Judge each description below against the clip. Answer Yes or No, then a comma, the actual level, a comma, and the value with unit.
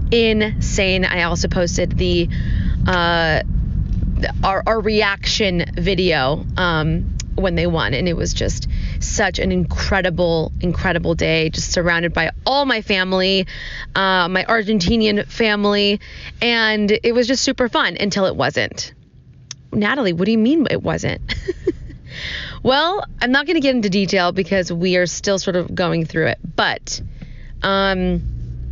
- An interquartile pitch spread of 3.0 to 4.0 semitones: No, average, 4.6 semitones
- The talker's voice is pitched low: No, medium, 185 Hz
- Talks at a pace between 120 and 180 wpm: Yes, average, 140 wpm